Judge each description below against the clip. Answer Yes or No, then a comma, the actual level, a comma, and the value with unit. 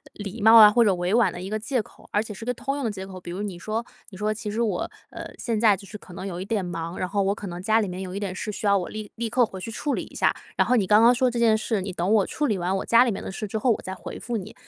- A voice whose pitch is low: No, high, 210 Hz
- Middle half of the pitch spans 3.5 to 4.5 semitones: No, average, 3.1 semitones